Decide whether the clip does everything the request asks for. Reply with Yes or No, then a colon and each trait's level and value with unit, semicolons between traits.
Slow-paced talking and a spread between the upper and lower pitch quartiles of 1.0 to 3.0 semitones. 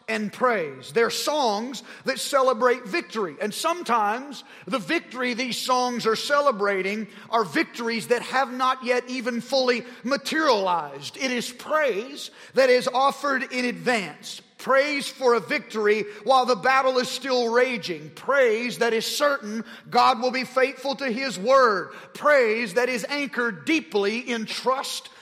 No: average, 145 wpm; average, 2.7 semitones